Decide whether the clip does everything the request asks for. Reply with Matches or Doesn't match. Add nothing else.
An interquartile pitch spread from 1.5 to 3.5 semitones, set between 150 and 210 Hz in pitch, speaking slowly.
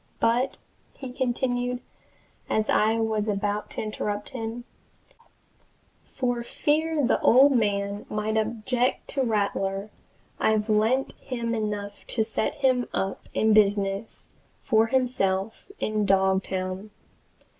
Doesn't match